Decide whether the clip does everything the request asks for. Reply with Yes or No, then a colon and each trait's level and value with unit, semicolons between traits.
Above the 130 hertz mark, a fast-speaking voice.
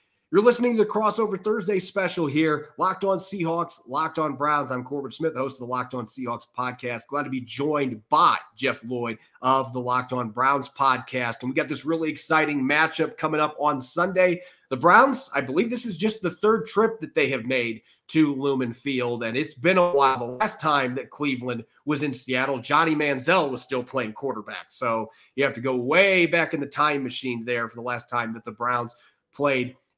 Yes: medium, 140 Hz; fast, 210 wpm